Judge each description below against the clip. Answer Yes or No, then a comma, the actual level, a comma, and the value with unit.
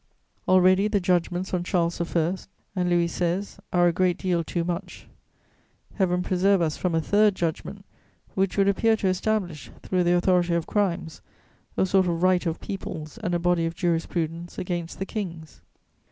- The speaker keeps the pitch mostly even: Yes, narrow, 1.8 semitones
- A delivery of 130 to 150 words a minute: No, average, 170 wpm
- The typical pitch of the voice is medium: Yes, medium, 180 Hz